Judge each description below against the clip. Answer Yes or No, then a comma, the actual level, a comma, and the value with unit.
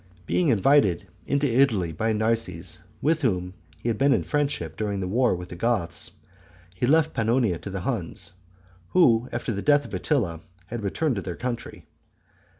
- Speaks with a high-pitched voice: No, low, 115 Hz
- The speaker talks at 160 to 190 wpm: Yes, average, 170 wpm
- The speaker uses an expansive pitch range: Yes, wide, 6.5 semitones